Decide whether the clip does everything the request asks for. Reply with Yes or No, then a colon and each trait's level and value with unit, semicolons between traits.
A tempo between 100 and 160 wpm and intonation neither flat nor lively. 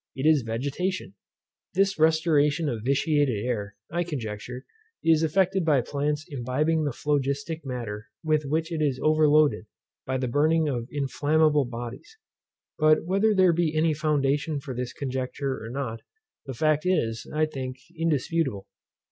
Yes: average, 145 wpm; average, 3.7 semitones